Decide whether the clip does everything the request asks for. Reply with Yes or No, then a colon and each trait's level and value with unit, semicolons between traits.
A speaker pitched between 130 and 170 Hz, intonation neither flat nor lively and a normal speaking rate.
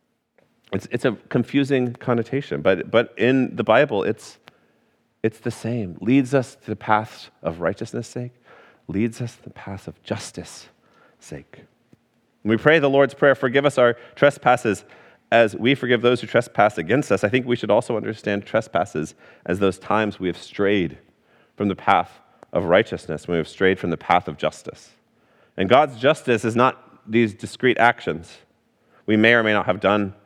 No: low, 115 Hz; average, 3.4 semitones; average, 180 wpm